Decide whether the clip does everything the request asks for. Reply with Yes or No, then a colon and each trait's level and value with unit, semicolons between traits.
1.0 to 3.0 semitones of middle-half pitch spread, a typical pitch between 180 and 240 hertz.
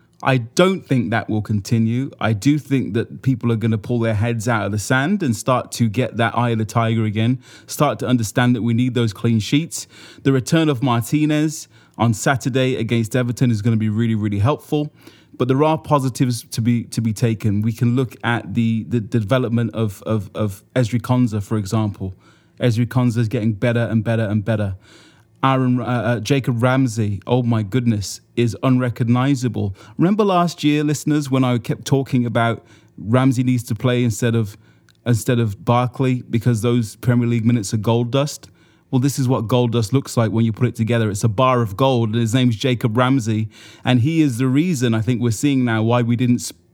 No: narrow, 2.4 semitones; low, 120 Hz